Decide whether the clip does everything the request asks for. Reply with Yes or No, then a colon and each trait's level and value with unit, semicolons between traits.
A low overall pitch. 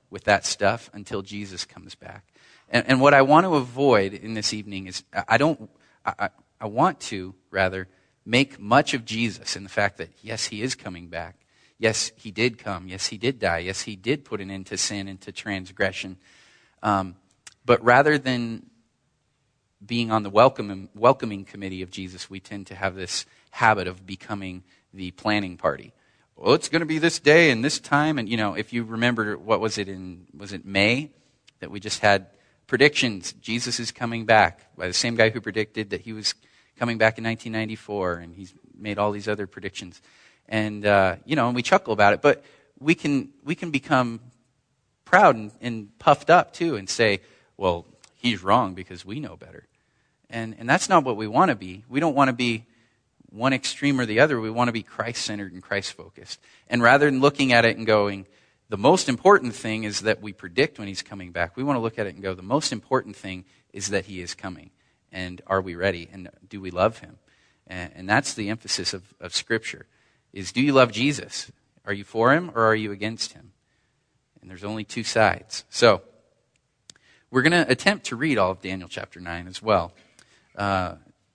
Yes: low, 105 Hz